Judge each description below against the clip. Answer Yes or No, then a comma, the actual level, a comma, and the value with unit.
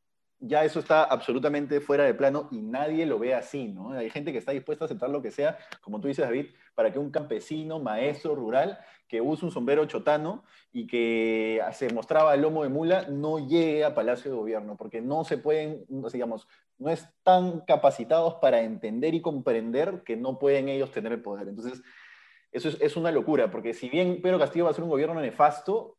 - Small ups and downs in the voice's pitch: No, average, 4.3 semitones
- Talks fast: Yes, fast, 210 wpm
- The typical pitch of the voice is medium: Yes, medium, 155 Hz